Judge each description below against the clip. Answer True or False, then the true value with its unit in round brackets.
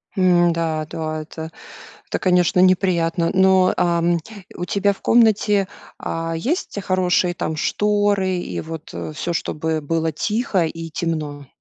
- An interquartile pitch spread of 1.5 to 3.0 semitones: True (2.7 semitones)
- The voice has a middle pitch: True (175 Hz)